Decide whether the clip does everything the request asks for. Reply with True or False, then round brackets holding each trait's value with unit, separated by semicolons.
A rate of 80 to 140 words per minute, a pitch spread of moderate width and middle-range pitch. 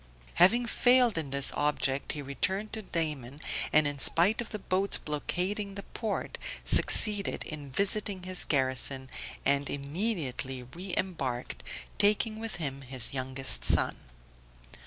False (135 wpm; 6.8 semitones; 160 Hz)